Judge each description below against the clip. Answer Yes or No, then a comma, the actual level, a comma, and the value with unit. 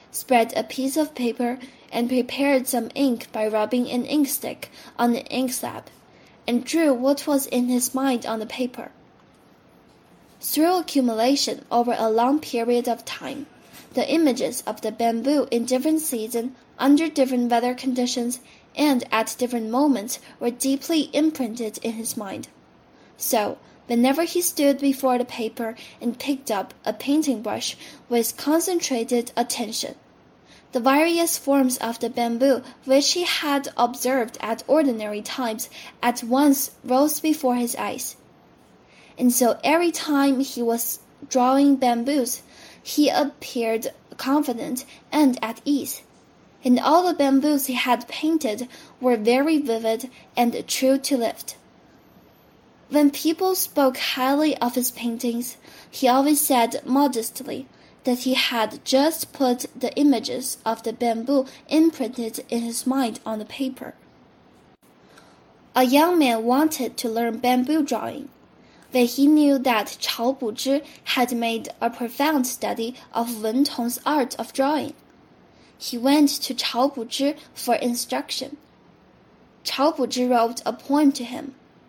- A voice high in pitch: Yes, very high, 255 Hz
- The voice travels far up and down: No, average, 3.0 semitones